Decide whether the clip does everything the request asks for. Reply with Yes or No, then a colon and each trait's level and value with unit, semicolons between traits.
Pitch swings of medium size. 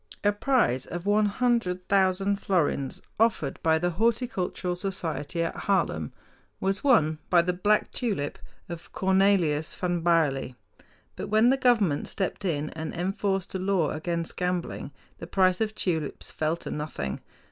Yes: average, 3.9 semitones